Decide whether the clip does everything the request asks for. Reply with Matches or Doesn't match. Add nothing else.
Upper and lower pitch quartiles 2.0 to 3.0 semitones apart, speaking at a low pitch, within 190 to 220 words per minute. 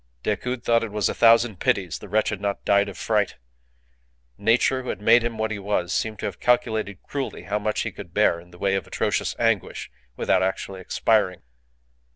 Matches